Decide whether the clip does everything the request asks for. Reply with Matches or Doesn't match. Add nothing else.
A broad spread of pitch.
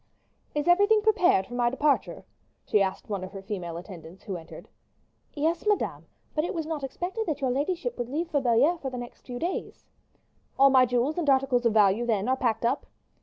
Matches